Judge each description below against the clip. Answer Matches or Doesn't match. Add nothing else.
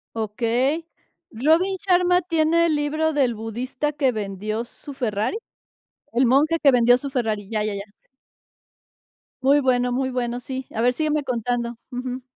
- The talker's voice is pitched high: Matches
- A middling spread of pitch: Matches